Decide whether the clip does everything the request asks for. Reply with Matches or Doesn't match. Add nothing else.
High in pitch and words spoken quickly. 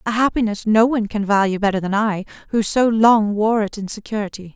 Matches